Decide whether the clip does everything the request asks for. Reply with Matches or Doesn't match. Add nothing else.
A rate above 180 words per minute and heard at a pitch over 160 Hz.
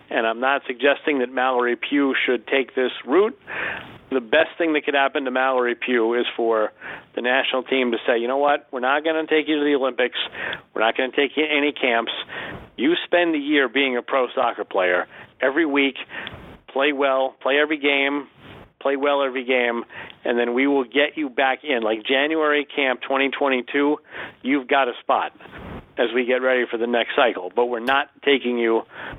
Doesn't match